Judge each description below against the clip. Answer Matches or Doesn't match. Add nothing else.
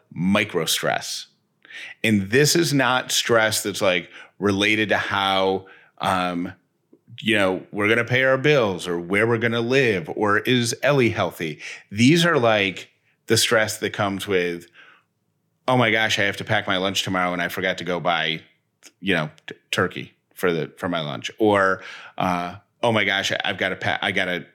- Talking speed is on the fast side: Doesn't match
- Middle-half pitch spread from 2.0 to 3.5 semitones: Doesn't match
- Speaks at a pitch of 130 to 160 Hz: Doesn't match